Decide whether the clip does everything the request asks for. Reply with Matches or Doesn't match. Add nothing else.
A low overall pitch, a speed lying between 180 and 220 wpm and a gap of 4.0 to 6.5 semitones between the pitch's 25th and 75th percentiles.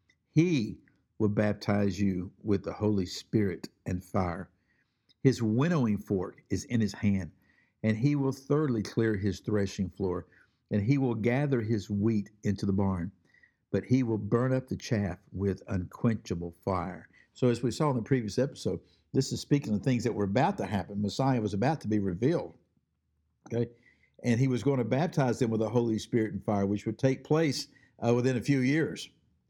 Matches